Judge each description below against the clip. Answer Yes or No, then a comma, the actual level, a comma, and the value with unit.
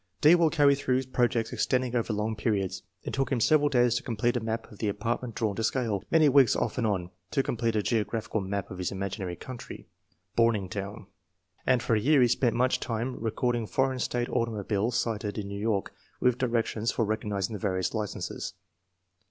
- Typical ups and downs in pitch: Yes, average, 3.2 semitones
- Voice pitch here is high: No, low, 115 Hz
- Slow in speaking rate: No, average, 195 wpm